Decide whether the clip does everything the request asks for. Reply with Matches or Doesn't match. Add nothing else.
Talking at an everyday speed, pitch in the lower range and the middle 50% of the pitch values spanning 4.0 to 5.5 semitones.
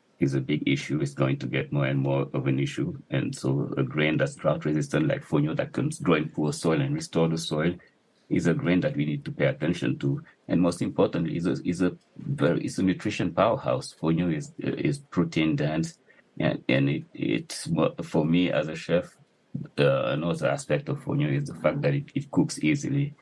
Doesn't match